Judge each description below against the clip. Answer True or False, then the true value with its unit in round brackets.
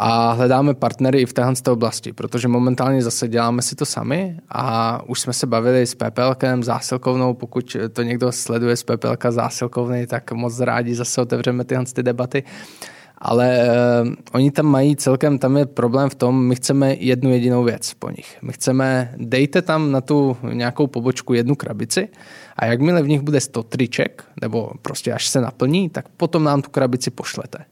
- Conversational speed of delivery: False (175 wpm)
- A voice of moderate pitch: False (125 Hz)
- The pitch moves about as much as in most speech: False (2.1 semitones)